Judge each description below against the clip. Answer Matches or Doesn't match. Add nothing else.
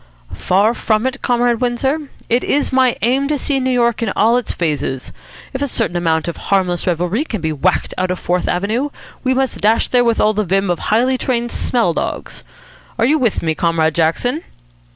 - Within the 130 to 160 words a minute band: Doesn't match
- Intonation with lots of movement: Matches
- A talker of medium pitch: Doesn't match